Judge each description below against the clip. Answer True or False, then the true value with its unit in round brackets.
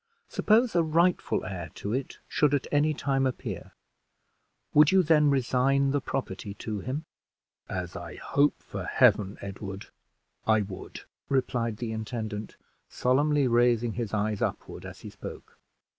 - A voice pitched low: True (125 Hz)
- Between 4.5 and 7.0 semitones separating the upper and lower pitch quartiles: True (5.2 semitones)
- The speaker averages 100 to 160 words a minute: True (145 wpm)